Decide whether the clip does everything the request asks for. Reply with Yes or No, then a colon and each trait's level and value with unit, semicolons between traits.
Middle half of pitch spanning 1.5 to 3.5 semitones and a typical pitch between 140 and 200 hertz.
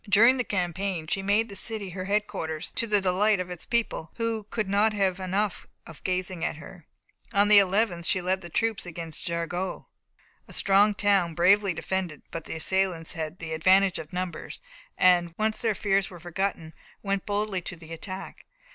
Yes: average, 2.9 semitones; high, 190 Hz